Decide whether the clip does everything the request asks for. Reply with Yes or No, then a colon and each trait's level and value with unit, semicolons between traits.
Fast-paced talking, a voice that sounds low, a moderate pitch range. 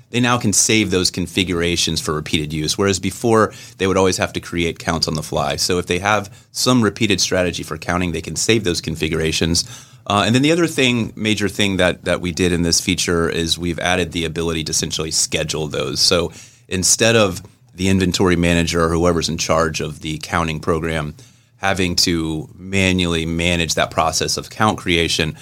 No: average, 195 wpm; very low, 90 Hz; average, 3.7 semitones